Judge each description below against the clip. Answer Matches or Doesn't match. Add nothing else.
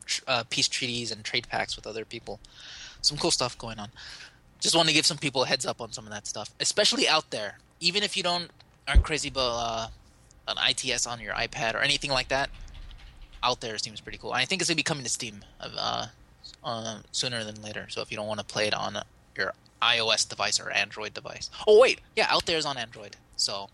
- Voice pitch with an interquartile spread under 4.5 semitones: Doesn't match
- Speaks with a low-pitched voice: Matches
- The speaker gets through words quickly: Matches